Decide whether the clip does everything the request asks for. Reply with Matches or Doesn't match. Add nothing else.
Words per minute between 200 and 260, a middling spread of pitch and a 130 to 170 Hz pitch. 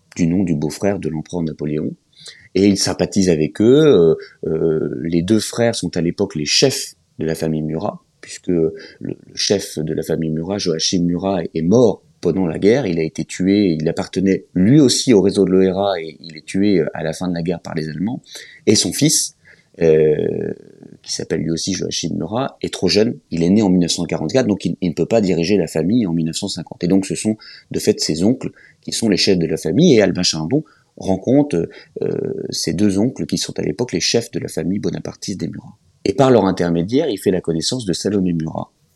Doesn't match